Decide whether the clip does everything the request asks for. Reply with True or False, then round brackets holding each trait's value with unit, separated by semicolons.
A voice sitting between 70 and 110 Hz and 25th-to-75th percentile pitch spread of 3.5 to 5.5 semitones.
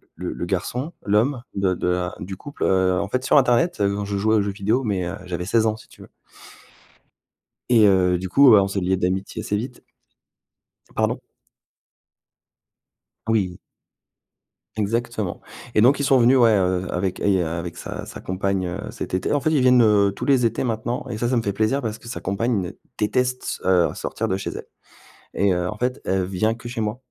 True (105 Hz; 4.2 semitones)